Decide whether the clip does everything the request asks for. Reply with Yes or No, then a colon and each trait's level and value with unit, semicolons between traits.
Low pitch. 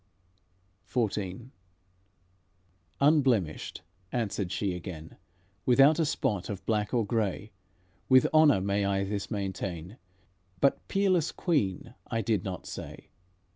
Yes: low, 105 Hz